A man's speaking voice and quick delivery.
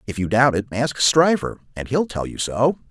Yes: male; fast, 230 wpm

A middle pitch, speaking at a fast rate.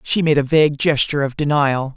Yes: medium, 145 Hz; fast, 215 wpm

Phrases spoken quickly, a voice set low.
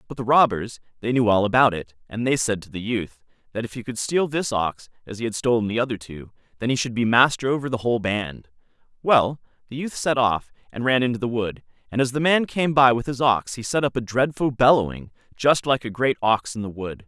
Yes: fast, 245 wpm; low, 120 Hz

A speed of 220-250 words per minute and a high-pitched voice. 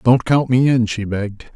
No: fast, 230 wpm; low, 120 Hz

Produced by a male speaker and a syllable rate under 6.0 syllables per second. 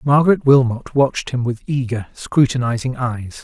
Yes: male; 5.0 syllables/s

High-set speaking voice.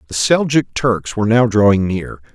No: low, 115 Hz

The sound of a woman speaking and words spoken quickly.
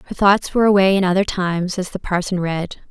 Yes: female; fast, 225 wpm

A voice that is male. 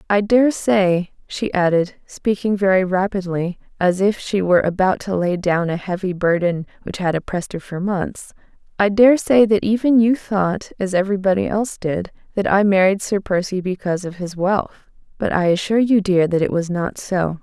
No: female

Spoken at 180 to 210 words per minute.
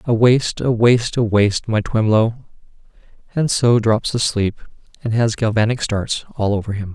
No: average, 165 wpm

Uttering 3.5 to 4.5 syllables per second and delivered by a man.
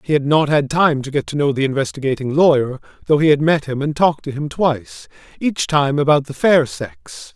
No: 5.4 syllables/s; male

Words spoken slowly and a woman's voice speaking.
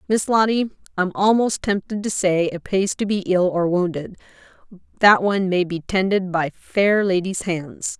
No: average, 175 wpm; female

